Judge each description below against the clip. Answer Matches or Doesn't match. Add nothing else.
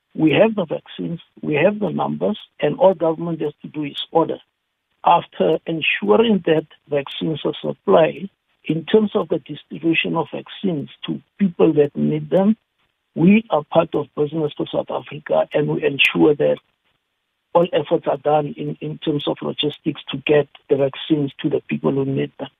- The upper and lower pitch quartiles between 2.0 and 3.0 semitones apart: Matches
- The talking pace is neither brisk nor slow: Matches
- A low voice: Doesn't match